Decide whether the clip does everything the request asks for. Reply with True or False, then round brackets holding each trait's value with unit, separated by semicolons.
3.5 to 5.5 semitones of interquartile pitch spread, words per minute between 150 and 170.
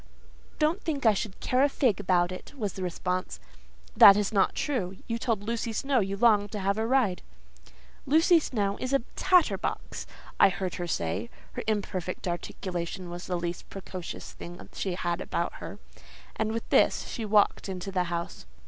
False (4.2 semitones; 180 wpm)